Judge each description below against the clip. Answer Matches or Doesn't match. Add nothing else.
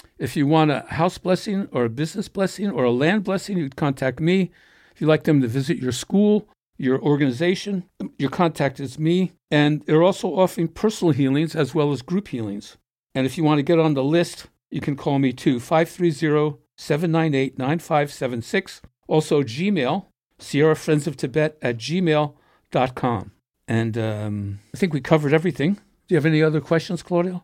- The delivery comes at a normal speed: Matches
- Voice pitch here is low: Doesn't match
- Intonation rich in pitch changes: Doesn't match